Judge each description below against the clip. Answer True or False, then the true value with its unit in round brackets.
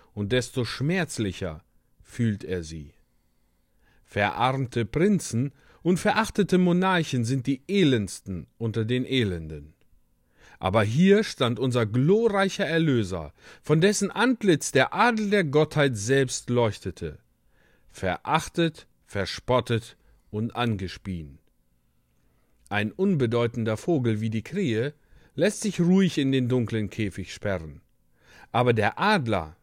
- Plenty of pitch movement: True (8.4 semitones)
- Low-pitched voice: True (120 Hz)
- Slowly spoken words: True (105 wpm)